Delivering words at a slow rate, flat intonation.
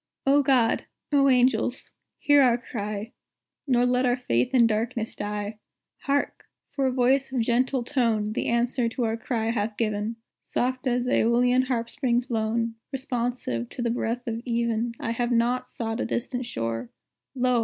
No: average, 160 wpm; narrow, 2.0 semitones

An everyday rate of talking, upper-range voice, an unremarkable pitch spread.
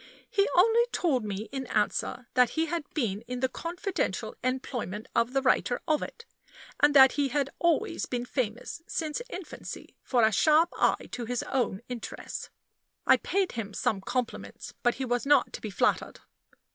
Yes: average, 170 wpm; very high, 260 Hz; average, 4.7 semitones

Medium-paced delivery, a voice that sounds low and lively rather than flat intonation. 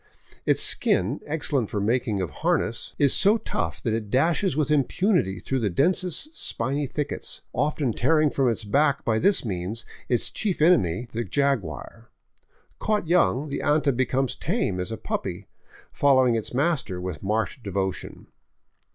Yes: average, 160 wpm; low, 130 Hz; wide, 6.1 semitones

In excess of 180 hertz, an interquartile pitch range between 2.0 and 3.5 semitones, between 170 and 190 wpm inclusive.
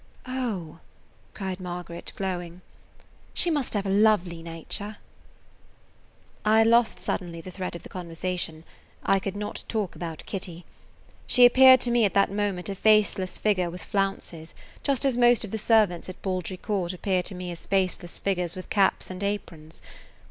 No: high, 190 Hz; average, 3.2 semitones; average, 160 wpm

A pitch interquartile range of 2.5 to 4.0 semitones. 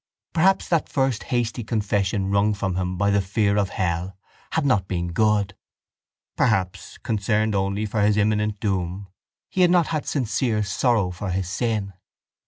Yes: average, 2.9 semitones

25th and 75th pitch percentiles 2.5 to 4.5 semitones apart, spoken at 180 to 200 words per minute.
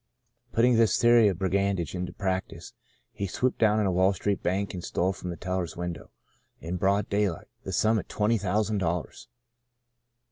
Yes: average, 2.9 semitones; average, 185 wpm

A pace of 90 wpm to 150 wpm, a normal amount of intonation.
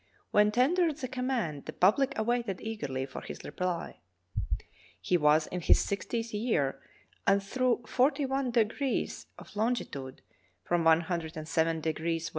No: slow, 135 wpm; wide, 7.4 semitones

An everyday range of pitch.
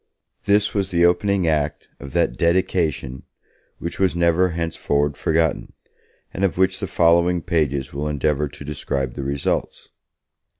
Yes: average, 3.5 semitones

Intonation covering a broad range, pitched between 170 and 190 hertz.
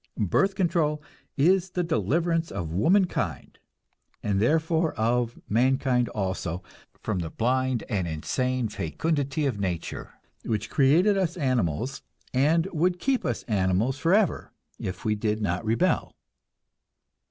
No: wide, 7.9 semitones; low, 130 Hz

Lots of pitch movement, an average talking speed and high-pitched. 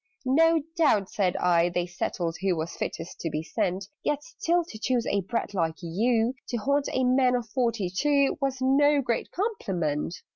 Yes: wide, 7.5 semitones; average, 180 wpm; high, 230 Hz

